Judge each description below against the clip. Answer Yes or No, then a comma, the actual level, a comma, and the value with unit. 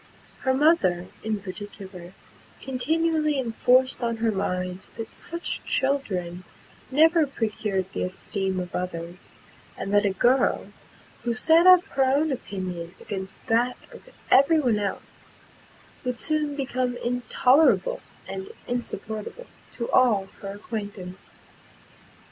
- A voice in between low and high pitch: No, high, 230 Hz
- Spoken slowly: Yes, slow, 120 wpm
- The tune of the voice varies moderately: No, wide, 6.1 semitones